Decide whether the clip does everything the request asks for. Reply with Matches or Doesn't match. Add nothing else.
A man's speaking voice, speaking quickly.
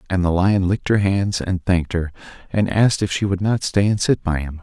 Matches